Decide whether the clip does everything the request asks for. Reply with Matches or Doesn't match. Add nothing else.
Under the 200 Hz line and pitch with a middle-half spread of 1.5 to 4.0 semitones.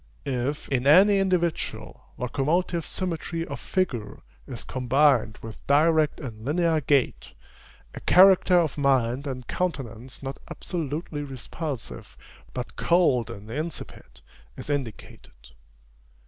Doesn't match